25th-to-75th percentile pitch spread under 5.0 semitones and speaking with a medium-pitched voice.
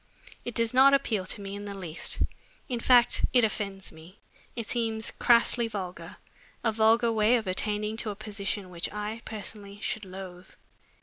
No: average, 2.8 semitones; high, 215 Hz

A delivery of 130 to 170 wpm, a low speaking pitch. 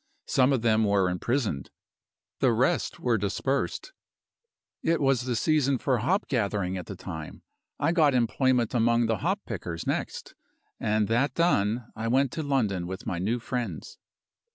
Yes: average, 155 wpm; low, 115 Hz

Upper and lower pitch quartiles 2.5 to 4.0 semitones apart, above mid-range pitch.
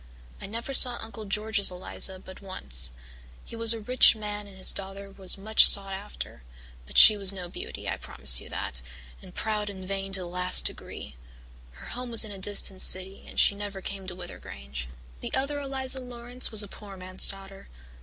Yes: average, 2.8 semitones; high, 195 Hz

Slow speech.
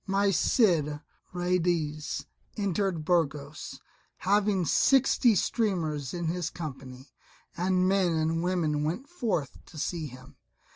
Yes: slow, 110 wpm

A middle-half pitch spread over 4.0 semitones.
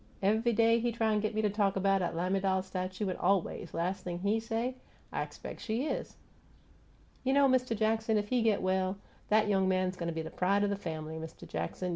No: average, 3.2 semitones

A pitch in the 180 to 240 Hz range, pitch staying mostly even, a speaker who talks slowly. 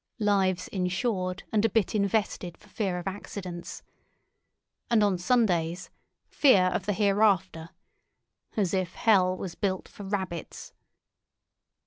Yes: high, 190 Hz; narrow, 2.3 semitones; slow, 115 wpm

